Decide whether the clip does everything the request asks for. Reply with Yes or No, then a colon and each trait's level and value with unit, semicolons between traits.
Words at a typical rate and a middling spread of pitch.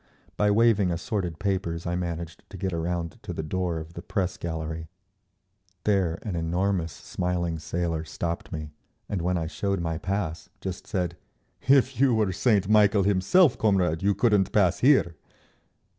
Yes: average, 160 wpm; average, 3.3 semitones